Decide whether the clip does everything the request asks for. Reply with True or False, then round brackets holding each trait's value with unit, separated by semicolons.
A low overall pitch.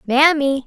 False (280 Hz)